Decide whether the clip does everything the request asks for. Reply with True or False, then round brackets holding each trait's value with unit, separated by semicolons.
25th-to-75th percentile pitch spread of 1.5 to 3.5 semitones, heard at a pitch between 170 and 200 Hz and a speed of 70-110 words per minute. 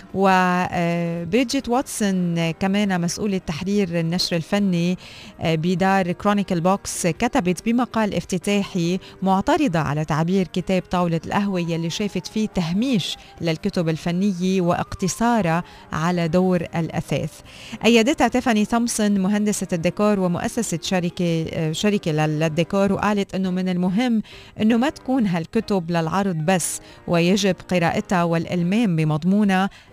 True (3.1 semitones; 185 Hz; 105 wpm)